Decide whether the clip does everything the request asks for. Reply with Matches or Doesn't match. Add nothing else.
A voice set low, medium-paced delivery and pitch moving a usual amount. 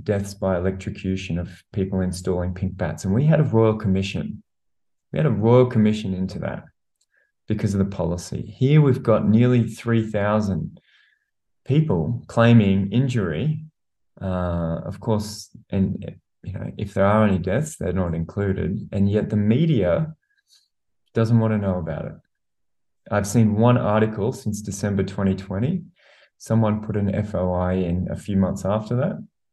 Matches